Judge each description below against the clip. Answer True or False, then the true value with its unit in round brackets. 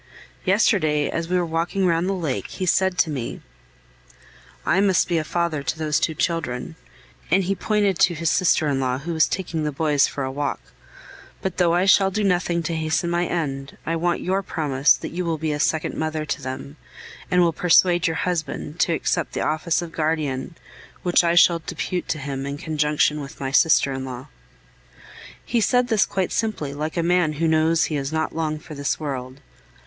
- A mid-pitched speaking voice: True (160 Hz)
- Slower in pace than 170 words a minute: False (205 wpm)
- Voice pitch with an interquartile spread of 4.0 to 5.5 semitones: False (3.1 semitones)